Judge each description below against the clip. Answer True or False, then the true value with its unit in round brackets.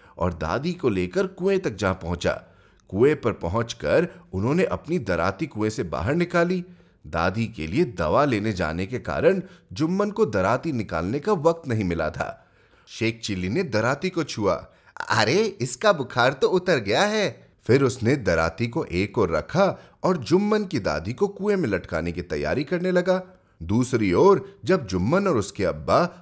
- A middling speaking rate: True (170 wpm)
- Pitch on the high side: False (145 Hz)